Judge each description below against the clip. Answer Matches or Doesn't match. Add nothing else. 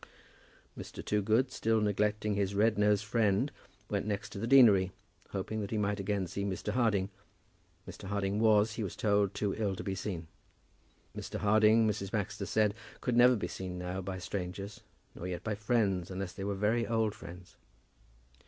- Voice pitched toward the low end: Matches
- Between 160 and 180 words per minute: Matches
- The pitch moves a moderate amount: Doesn't match